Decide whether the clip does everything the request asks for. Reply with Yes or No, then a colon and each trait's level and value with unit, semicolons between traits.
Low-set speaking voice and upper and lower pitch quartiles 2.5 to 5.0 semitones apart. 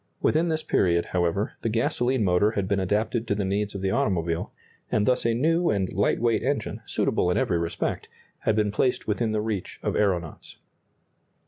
Yes: low, 105 Hz; average, 3.8 semitones